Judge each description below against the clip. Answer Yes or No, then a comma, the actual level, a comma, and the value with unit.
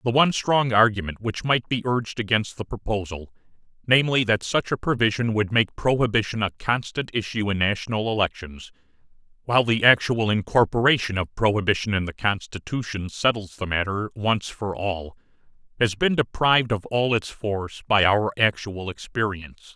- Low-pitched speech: Yes, low, 110 Hz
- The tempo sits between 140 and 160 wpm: Yes, average, 150 wpm